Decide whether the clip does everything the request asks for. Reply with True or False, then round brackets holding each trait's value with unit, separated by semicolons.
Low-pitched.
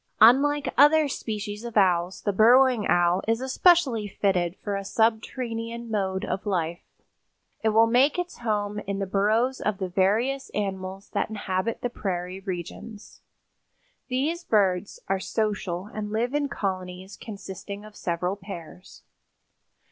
False (210 Hz)